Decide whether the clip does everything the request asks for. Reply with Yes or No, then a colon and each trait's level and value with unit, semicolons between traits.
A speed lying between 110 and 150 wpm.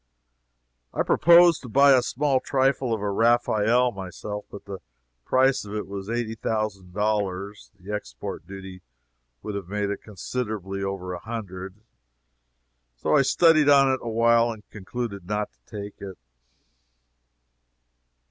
Yes: average, 145 wpm